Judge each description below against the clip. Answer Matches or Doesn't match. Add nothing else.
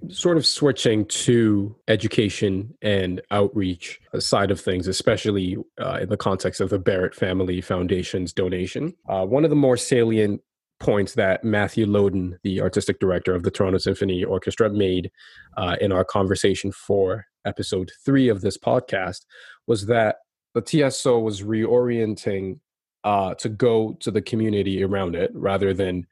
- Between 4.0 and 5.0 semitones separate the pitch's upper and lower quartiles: Doesn't match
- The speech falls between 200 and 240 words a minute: Doesn't match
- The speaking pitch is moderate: Doesn't match